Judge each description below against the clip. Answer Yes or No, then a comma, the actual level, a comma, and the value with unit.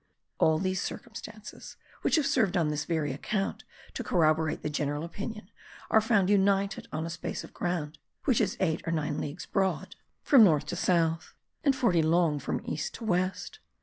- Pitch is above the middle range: No, medium, 180 Hz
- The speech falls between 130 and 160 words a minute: No, average, 180 wpm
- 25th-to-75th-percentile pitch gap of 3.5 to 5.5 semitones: Yes, average, 4.6 semitones